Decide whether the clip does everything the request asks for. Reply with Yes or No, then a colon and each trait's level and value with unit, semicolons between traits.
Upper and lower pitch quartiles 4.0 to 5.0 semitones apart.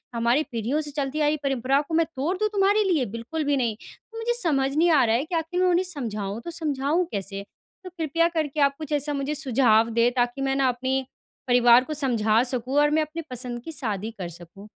Yes: average, 4.7 semitones